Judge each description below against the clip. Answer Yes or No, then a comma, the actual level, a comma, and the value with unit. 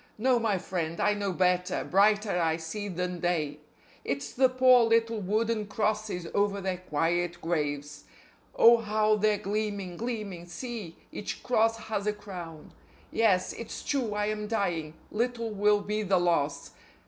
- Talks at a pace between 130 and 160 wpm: Yes, average, 150 wpm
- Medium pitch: No, high, 205 Hz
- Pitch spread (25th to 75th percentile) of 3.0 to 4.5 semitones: Yes, average, 3.7 semitones